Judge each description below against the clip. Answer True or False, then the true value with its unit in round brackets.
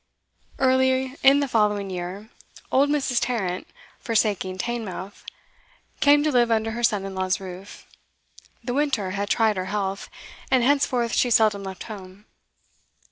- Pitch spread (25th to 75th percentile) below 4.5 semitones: False (4.8 semitones)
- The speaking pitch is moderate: False (220 Hz)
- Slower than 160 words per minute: True (140 wpm)